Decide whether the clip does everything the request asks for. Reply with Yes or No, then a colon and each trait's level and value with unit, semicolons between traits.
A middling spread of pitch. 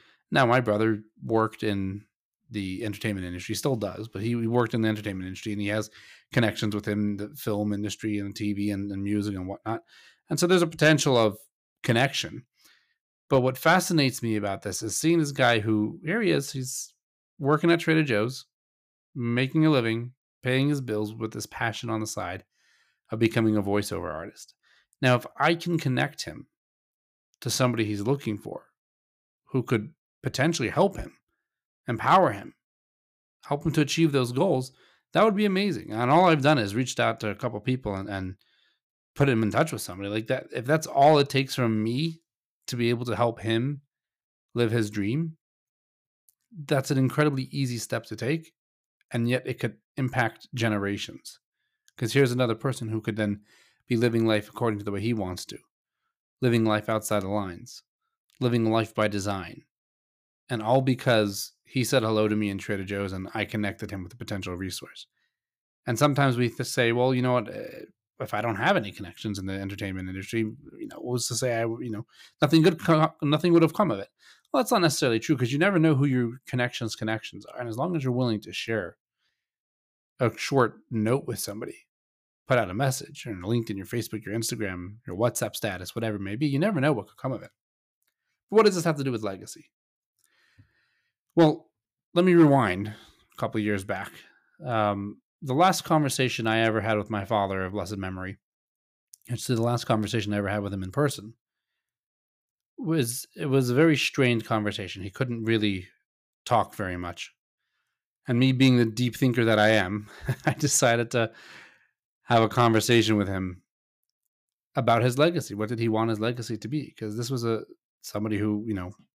Yes: average, 4.2 semitones